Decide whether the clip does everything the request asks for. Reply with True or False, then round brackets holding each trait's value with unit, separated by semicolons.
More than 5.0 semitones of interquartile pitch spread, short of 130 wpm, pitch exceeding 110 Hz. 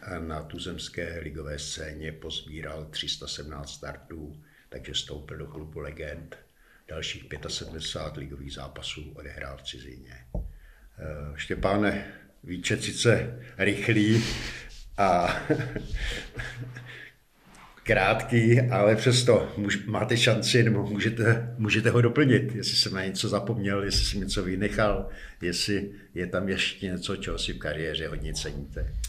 False (5.6 semitones; 115 wpm; 90 Hz)